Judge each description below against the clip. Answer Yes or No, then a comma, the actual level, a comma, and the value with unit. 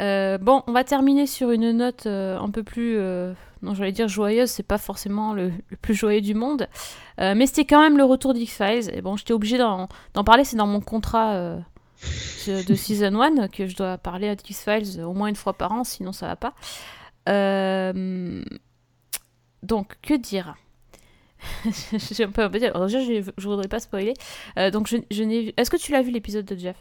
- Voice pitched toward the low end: No, high, 210 Hz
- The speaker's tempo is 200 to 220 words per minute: Yes, average, 205 wpm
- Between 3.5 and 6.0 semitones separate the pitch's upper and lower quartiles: No, average, 3.1 semitones